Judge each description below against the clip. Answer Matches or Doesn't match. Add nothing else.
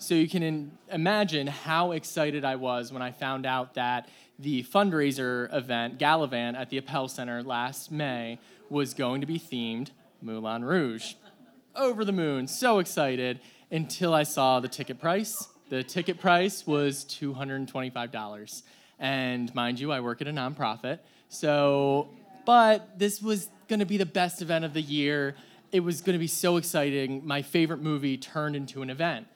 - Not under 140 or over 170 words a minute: Matches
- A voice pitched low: Doesn't match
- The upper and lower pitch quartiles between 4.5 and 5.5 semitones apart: Matches